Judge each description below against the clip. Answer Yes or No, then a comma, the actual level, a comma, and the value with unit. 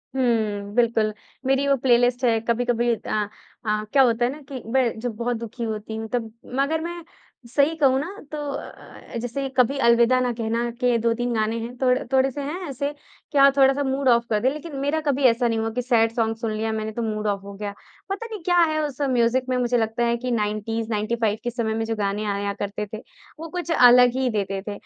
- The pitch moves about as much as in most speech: Yes, average, 3.2 semitones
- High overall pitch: Yes, high, 240 Hz